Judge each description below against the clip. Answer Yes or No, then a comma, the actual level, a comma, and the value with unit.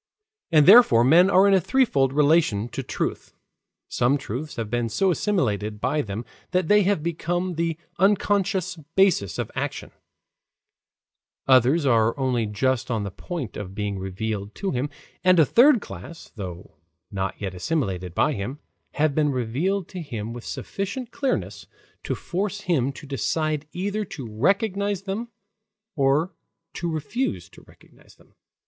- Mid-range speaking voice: Yes, medium, 150 Hz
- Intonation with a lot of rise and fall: Yes, wide, 8.4 semitones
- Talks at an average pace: Yes, average, 150 wpm